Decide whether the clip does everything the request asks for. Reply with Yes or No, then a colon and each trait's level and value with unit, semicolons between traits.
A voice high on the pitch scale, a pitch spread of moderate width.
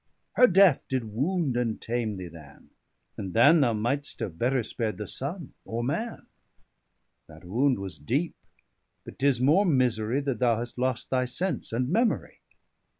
No: low, 125 Hz; average, 4.4 semitones